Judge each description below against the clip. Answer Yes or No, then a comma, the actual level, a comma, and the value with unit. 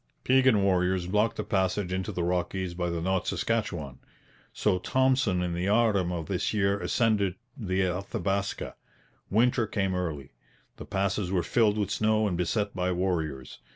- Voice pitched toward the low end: Yes, very low, 95 Hz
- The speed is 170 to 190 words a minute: No, average, 155 wpm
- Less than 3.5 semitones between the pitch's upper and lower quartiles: Yes, average, 2.8 semitones